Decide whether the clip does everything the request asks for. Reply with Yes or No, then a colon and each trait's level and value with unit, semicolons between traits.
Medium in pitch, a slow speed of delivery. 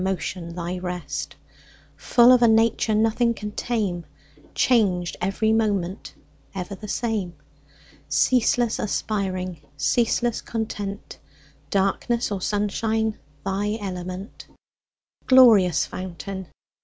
No: high, 205 Hz; slow, 95 wpm